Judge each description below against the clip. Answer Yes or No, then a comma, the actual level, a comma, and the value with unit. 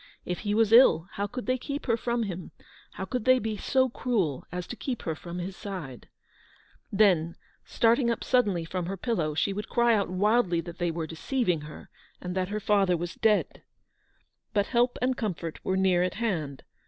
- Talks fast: No, average, 195 wpm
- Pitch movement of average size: Yes, average, 5.0 semitones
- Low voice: No, high, 200 Hz